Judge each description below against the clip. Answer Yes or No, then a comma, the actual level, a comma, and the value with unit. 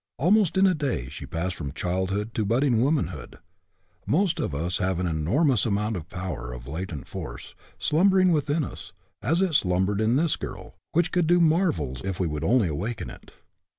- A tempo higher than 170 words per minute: Yes, average, 185 wpm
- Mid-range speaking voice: No, low, 105 Hz